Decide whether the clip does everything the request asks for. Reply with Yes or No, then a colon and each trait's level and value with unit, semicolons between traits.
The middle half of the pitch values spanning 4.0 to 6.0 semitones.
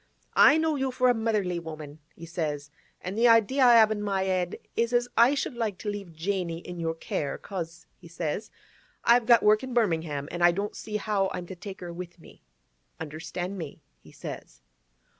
Yes: average, 5.2 semitones